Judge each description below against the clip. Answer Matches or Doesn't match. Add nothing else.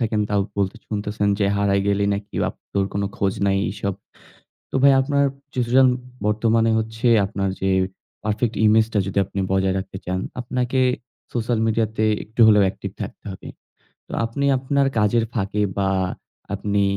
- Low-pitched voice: Matches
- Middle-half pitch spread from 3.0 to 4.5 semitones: Doesn't match